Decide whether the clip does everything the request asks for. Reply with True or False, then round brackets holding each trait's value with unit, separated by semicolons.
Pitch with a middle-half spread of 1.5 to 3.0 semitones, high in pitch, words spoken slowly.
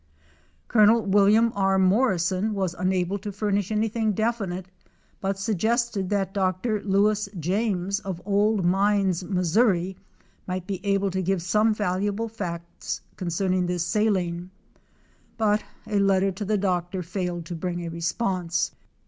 True (2.6 semitones; 195 Hz; 130 wpm)